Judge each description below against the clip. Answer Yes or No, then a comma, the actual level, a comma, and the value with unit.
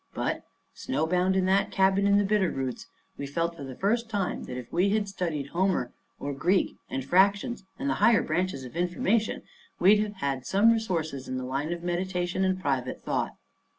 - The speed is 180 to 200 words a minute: Yes, average, 190 wpm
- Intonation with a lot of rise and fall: Yes, wide, 5.7 semitones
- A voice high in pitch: No, medium, 180 Hz